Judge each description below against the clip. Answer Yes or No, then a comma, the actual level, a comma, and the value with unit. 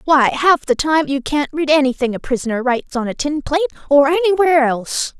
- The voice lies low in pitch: No, very high, 290 Hz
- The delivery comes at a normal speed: No, fast, 210 wpm